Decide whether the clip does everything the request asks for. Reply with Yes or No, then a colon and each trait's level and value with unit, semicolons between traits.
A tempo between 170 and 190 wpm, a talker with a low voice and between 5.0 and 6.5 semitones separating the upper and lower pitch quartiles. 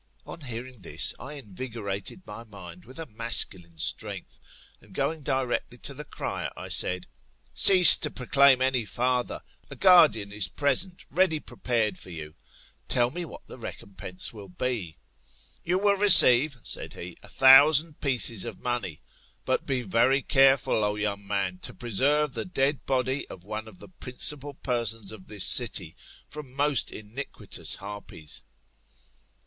No: average, 155 wpm; low, 125 Hz; average, 5.3 semitones